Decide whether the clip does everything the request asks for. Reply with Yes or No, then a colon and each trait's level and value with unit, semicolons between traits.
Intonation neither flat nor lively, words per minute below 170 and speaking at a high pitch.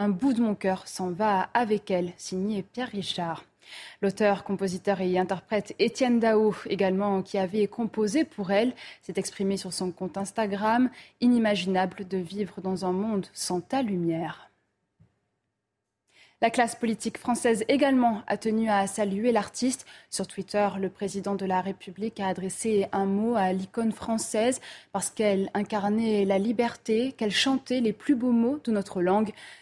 Yes: average, 3.1 semitones; average, 155 wpm; high, 205 Hz